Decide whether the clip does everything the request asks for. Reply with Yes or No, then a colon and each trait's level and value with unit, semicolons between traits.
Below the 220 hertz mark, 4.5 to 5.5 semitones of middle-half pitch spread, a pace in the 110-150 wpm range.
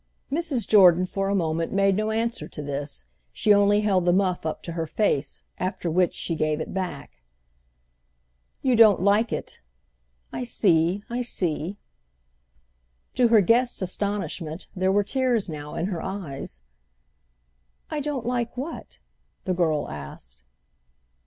Yes: high, 190 Hz; average, 5.0 semitones; average, 145 wpm